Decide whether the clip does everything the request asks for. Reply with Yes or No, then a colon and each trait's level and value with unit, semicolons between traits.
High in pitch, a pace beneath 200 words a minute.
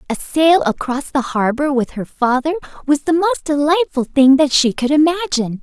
Yes: very high, 290 Hz; average, 180 wpm